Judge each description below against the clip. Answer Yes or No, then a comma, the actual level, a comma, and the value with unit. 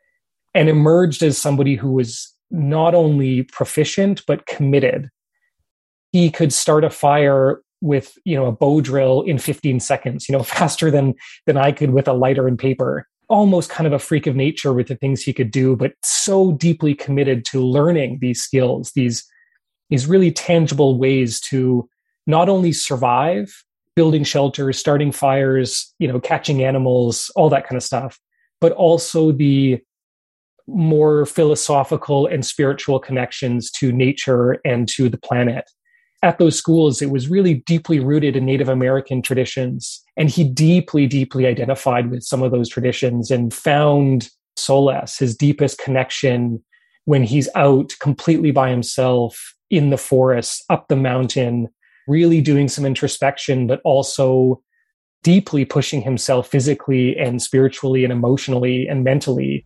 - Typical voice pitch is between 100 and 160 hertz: Yes, low, 135 Hz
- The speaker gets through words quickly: No, average, 150 wpm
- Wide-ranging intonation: No, average, 2.9 semitones